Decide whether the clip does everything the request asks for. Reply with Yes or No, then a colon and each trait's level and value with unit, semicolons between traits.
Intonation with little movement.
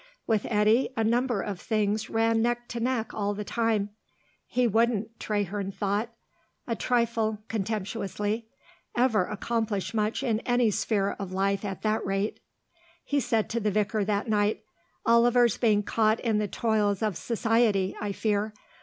Yes: narrow, 2.0 semitones